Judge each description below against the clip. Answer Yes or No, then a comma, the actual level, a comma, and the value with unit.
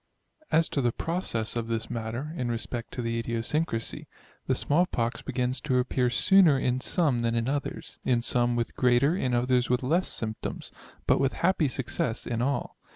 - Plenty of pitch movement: No, average, 3.2 semitones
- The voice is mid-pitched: No, low, 125 Hz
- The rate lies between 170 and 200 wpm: Yes, average, 180 wpm